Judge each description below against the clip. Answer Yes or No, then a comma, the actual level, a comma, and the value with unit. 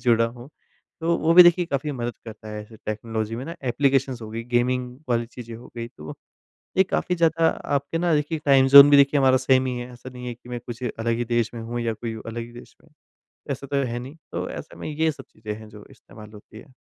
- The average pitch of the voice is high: No, low, 125 Hz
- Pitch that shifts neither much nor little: Yes, average, 3.4 semitones